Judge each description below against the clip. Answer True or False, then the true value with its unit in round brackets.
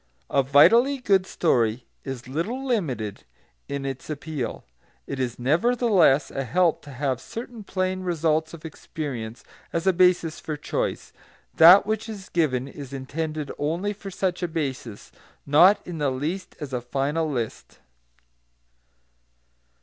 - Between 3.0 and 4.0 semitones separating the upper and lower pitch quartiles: False (5.5 semitones)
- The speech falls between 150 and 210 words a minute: False (140 wpm)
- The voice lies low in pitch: False (155 Hz)